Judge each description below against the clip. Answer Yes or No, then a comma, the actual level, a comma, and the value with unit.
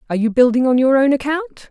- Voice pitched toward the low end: No, very high, 265 Hz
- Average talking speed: No, fast, 245 wpm